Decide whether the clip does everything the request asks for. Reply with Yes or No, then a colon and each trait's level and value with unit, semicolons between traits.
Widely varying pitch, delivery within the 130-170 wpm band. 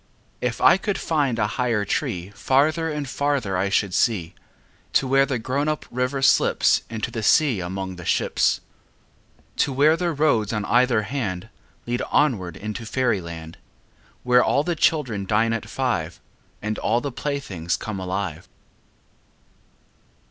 Yes: wide, 5.7 semitones; average, 150 wpm